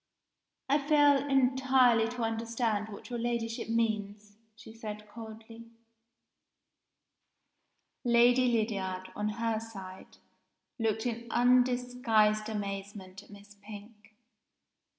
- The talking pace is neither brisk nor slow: No, slow, 95 wpm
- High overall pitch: Yes, high, 225 Hz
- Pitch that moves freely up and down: No, narrow, 2.5 semitones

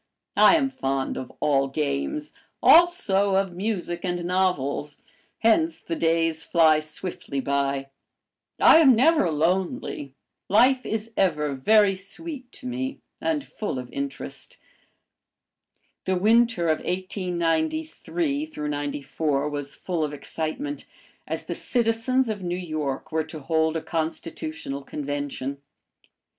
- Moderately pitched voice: Yes, medium, 175 Hz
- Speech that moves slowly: Yes, slow, 120 wpm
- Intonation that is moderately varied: No, wide, 7.6 semitones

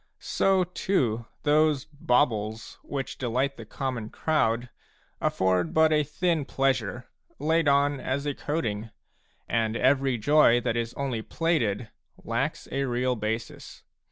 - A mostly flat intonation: No, average, 4.4 semitones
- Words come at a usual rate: No, slow, 130 wpm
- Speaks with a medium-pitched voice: No, low, 130 Hz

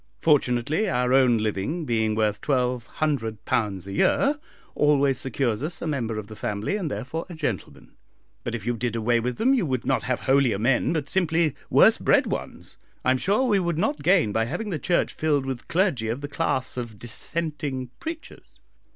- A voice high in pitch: No, low, 130 Hz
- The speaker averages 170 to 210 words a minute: Yes, average, 185 wpm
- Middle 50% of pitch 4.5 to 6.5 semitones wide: Yes, wide, 5.6 semitones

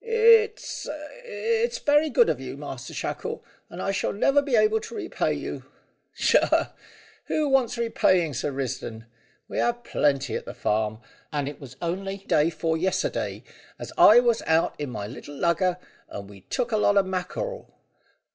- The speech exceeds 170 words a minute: No, average, 165 wpm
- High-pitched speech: Yes, high, 195 Hz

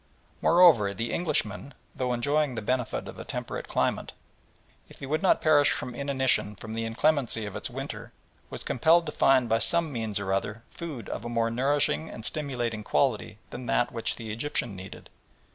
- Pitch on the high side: No, low, 120 Hz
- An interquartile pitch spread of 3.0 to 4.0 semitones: No, average, 4.4 semitones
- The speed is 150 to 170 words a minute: No, average, 180 wpm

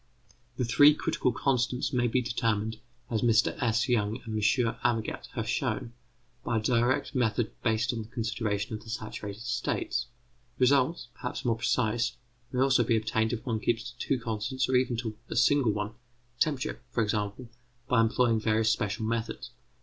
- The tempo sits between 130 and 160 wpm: No, average, 170 wpm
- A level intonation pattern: Yes, narrow, 2.2 semitones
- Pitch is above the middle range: No, low, 115 Hz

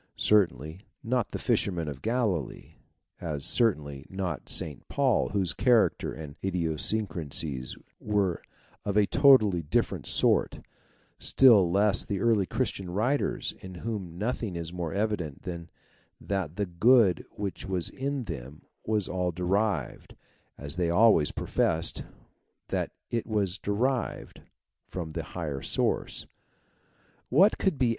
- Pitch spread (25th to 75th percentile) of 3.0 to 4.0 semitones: No, average, 4.8 semitones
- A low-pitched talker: Yes, very low, 95 Hz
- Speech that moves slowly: Yes, slow, 125 wpm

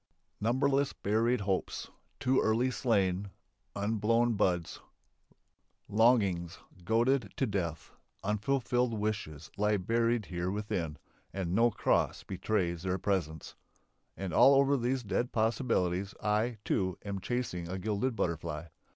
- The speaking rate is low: Yes, slow, 115 wpm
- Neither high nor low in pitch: No, low, 105 Hz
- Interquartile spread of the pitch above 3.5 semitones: Yes, average, 4.2 semitones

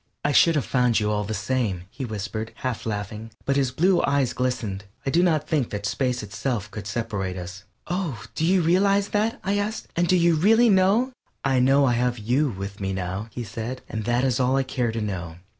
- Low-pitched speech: Yes, low, 125 Hz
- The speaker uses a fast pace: Yes, fast, 220 wpm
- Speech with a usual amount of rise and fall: No, wide, 6.9 semitones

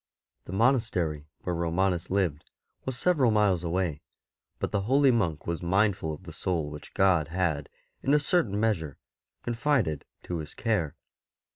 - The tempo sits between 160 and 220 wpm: No, average, 150 wpm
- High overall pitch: No, very low, 95 Hz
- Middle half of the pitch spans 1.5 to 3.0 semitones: No, wide, 5.6 semitones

